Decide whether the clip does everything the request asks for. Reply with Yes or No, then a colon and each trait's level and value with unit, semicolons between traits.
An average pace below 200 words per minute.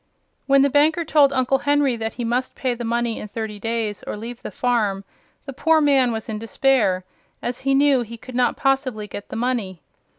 No: fast, 205 wpm